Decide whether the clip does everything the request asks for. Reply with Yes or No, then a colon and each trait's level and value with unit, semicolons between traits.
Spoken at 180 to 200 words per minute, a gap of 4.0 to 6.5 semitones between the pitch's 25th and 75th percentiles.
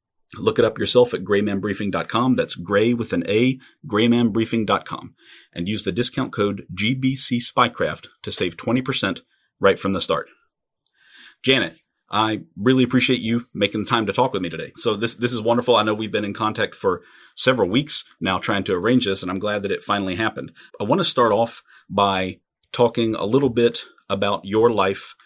No: average, 185 wpm; average, 3.1 semitones